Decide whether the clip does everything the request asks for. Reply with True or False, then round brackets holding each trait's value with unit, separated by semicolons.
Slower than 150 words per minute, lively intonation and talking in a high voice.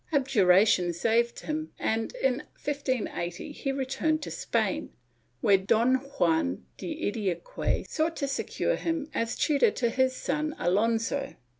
True (135 wpm; 6.1 semitones; 260 Hz)